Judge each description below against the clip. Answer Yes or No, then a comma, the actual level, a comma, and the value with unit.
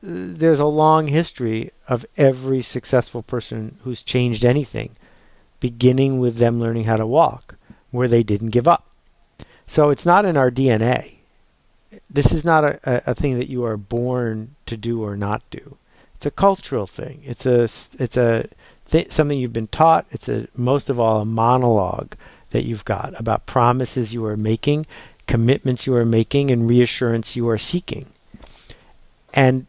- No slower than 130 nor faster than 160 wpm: No, average, 170 wpm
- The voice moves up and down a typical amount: Yes, average, 3.2 semitones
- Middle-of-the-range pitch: No, low, 125 Hz